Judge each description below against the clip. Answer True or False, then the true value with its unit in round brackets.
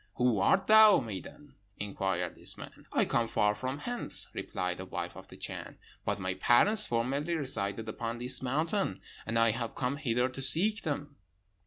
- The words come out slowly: False (175 wpm)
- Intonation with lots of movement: True (5.7 semitones)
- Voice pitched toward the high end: False (125 Hz)